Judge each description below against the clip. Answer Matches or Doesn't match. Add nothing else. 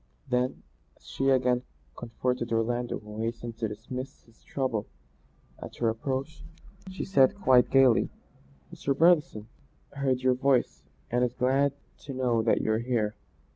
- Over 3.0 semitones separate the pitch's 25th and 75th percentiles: Doesn't match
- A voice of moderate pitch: Doesn't match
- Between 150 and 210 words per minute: Doesn't match